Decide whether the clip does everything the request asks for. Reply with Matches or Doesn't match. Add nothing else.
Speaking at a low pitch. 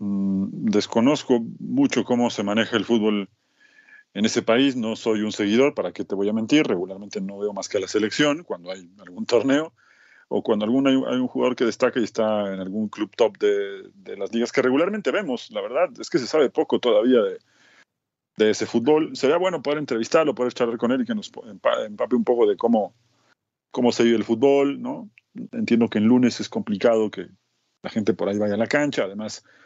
Matches